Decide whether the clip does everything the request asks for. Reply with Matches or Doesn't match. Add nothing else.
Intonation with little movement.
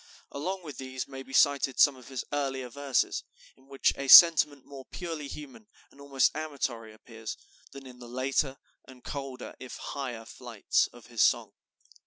Matches